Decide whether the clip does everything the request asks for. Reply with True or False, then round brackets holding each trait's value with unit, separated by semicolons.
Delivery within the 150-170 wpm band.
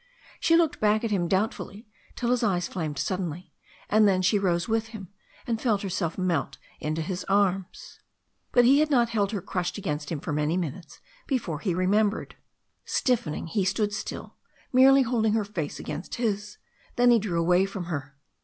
False (180 wpm)